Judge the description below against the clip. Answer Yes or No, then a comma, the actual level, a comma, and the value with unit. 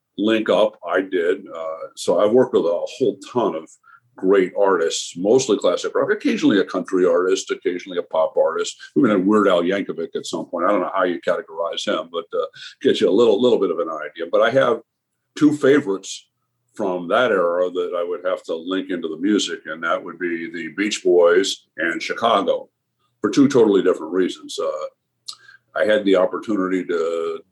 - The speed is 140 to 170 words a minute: No, average, 195 wpm